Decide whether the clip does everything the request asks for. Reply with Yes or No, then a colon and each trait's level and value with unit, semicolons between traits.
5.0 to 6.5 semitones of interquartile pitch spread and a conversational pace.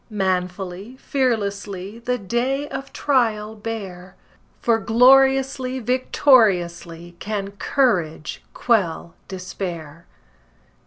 No: wide, 5.5 semitones; slow, 75 wpm